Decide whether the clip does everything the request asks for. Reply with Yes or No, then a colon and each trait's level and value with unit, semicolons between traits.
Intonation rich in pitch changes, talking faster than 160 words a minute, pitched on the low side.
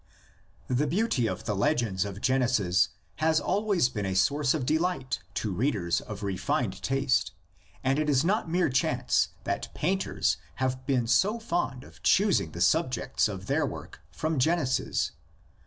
No: wide, 6.2 semitones; average, 155 wpm; low, 130 Hz